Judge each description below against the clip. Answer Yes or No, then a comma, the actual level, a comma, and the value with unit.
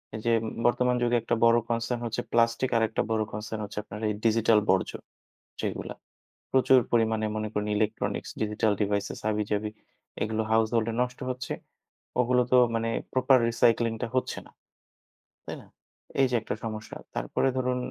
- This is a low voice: Yes, low, 115 Hz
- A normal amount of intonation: No, narrow, 2.0 semitones